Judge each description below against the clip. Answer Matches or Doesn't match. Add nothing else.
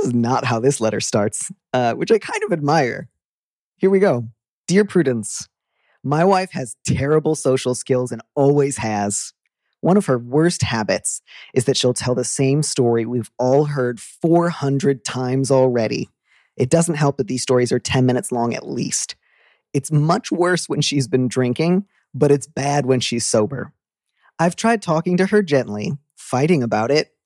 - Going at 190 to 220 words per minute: Doesn't match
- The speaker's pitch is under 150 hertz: Matches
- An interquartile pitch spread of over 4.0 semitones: Matches